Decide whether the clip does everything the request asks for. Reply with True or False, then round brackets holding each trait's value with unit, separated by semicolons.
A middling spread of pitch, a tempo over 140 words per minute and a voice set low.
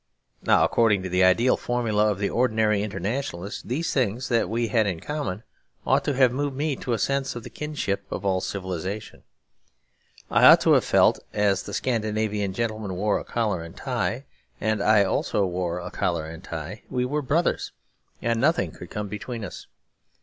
True (4.1 semitones; 185 wpm; 105 Hz)